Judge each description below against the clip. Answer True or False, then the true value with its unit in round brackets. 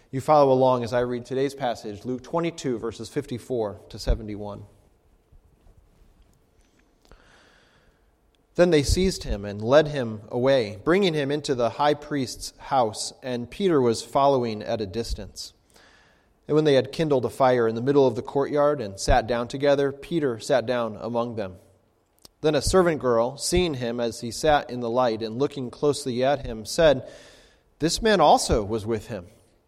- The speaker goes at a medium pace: True (165 wpm)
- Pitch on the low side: True (125 Hz)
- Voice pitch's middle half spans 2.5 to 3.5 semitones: False (4.1 semitones)